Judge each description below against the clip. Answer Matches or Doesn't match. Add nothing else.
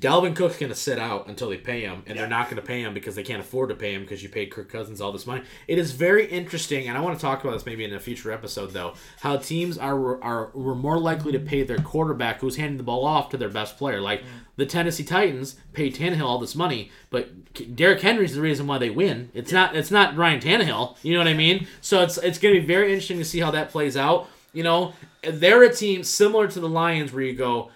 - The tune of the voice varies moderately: Doesn't match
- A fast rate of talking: Matches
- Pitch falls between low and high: Matches